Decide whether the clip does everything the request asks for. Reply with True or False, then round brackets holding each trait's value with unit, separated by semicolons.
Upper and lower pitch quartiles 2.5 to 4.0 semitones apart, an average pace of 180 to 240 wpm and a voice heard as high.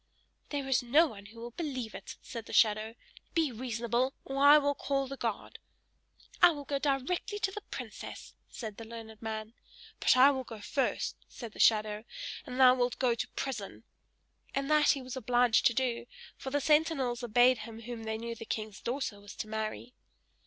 True (3.6 semitones; 190 wpm; 245 Hz)